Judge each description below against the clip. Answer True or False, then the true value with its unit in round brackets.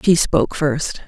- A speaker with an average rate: True (170 wpm)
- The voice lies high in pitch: False (145 Hz)